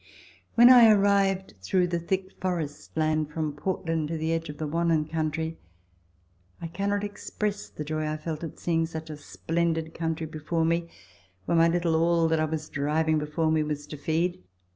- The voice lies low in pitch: No, medium, 165 Hz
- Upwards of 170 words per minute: Yes, average, 185 wpm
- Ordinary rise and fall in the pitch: No, narrow, 1.7 semitones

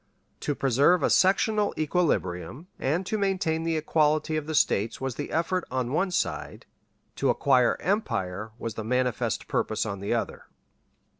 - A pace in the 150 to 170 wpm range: Yes, average, 155 wpm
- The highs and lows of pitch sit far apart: Yes, wide, 6.9 semitones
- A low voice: No, medium, 150 Hz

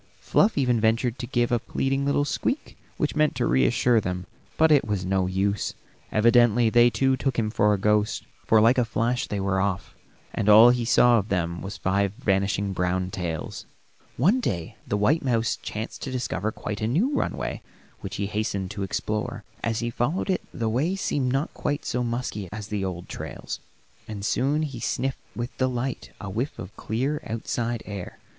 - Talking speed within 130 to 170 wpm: No, average, 190 wpm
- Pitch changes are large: No, average, 4.2 semitones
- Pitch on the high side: No, low, 115 Hz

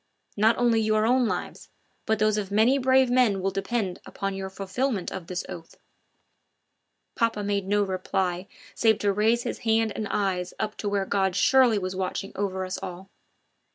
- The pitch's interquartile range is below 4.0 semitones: Yes, average, 2.8 semitones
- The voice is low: No, high, 205 Hz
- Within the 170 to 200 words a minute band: Yes, average, 175 wpm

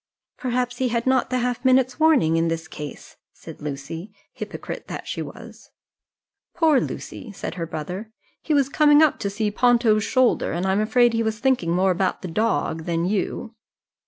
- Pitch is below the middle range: No, high, 220 Hz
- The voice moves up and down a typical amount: No, wide, 6.5 semitones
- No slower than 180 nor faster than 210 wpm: Yes, average, 185 wpm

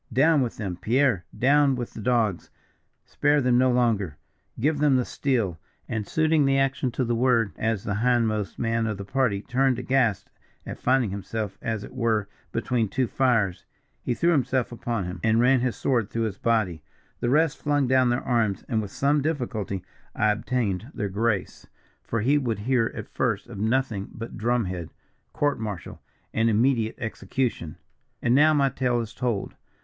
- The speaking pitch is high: No, low, 120 Hz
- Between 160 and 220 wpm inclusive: Yes, average, 180 wpm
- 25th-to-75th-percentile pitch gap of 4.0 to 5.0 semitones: No, average, 3.6 semitones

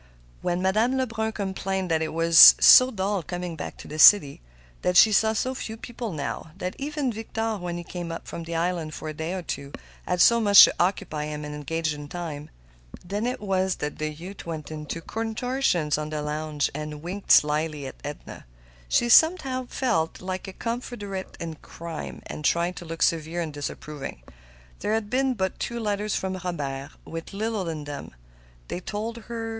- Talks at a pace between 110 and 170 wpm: No, average, 190 wpm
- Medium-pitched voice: Yes, medium, 180 Hz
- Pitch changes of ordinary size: No, wide, 5.8 semitones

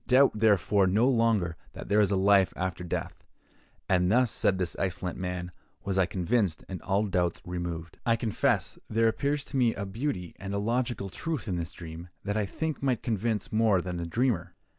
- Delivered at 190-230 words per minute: Yes, average, 195 wpm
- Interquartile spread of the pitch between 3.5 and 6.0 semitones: Yes, average, 4.2 semitones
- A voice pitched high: No, low, 100 Hz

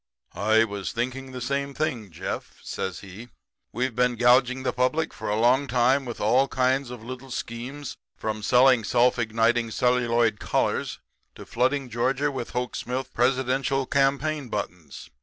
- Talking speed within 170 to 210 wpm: No, average, 155 wpm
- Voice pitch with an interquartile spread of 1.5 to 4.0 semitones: Yes, narrow, 2.4 semitones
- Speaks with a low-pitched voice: Yes, low, 125 Hz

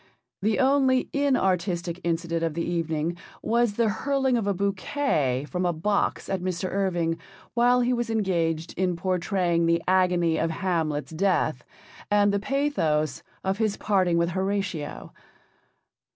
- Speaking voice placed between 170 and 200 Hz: Yes, medium, 185 Hz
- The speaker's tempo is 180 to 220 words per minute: No, average, 140 wpm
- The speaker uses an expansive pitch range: No, average, 3.9 semitones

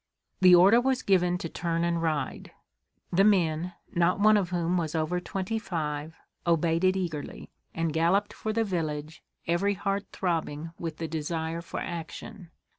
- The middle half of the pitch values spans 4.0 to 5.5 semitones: No, average, 2.8 semitones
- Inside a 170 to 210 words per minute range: No, average, 160 wpm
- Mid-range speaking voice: Yes, medium, 170 Hz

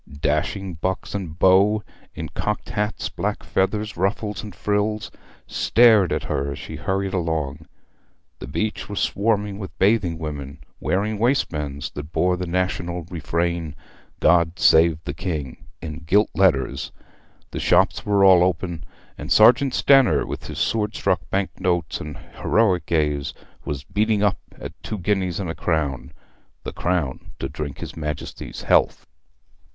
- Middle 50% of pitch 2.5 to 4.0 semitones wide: No, average, 4.6 semitones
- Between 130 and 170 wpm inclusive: Yes, average, 145 wpm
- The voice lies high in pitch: No, very low, 90 Hz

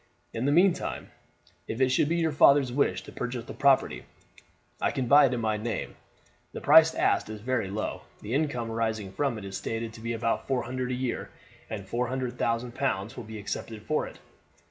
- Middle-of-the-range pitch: No, low, 120 Hz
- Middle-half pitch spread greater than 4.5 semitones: No, average, 3.5 semitones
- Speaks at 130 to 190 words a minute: No, fast, 205 wpm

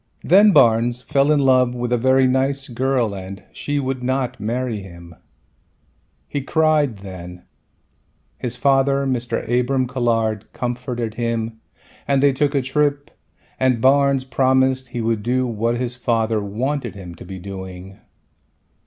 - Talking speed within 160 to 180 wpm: No, average, 145 wpm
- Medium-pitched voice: No, low, 125 Hz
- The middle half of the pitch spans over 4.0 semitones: No, average, 3.1 semitones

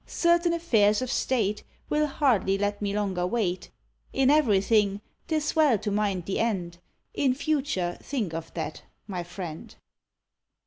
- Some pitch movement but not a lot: No, wide, 6.2 semitones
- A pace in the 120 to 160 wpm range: Yes, average, 140 wpm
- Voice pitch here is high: Yes, high, 210 Hz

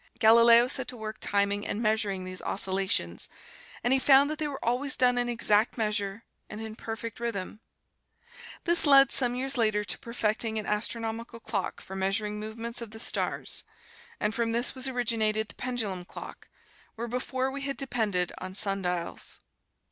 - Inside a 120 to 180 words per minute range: Yes, average, 165 wpm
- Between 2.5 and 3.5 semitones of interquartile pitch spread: Yes, average, 2.9 semitones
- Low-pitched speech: No, high, 225 Hz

